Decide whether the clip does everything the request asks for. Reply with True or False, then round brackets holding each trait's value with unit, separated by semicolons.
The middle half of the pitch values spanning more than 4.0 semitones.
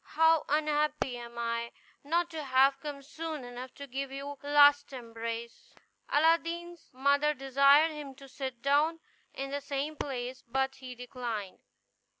False (2.9 semitones)